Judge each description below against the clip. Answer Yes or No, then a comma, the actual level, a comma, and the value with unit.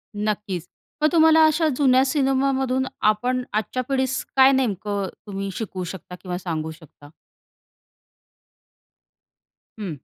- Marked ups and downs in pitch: Yes, wide, 5.9 semitones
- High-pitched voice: Yes, high, 220 Hz